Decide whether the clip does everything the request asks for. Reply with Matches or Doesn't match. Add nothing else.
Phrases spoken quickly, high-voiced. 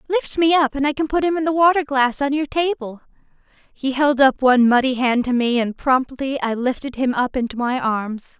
Matches